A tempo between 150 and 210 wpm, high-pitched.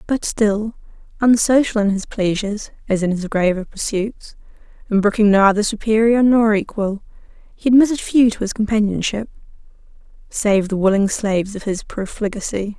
No: average, 140 wpm; high, 210 Hz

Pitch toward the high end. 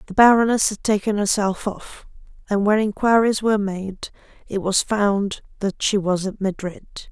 Yes: high, 205 Hz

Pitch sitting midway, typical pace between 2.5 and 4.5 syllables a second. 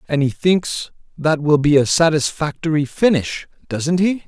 Yes: medium, 155 Hz; 4.4 syllables/s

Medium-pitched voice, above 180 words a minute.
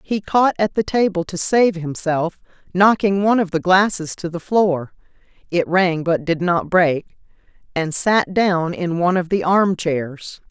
No: medium, 180 Hz; average, 160 wpm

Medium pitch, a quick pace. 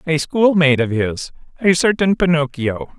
No: medium, 155 Hz; average, 140 wpm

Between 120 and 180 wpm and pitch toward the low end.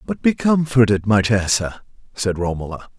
Yes: average, 140 wpm; low, 110 Hz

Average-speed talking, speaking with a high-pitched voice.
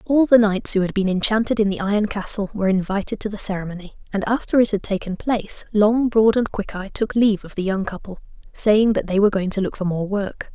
No: fast, 240 wpm; high, 205 Hz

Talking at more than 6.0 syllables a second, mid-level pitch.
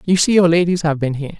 Yes: 7.1 syllables/s; medium, 165 Hz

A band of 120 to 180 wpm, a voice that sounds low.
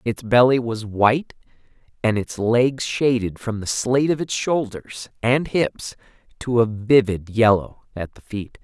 Yes: average, 160 wpm; low, 115 Hz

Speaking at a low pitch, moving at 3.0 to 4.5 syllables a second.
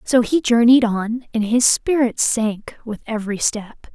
No: high, 230 Hz; 4.1 syllables/s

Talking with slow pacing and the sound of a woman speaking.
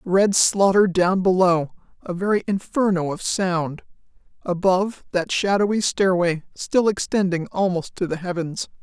Yes: slow, 130 wpm; female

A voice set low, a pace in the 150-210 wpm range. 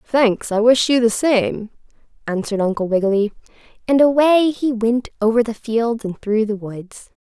No: high, 230 Hz; average, 165 wpm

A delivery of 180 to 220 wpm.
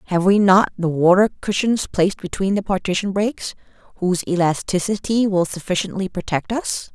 No: average, 145 wpm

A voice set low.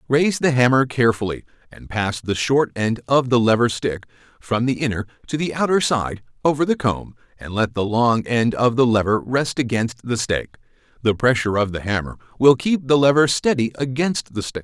Yes: low, 120 Hz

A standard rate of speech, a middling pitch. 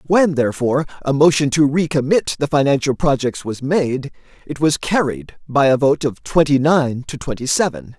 Yes: average, 175 wpm; medium, 145 Hz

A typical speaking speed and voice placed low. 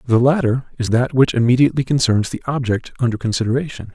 Yes: average, 165 wpm; low, 125 Hz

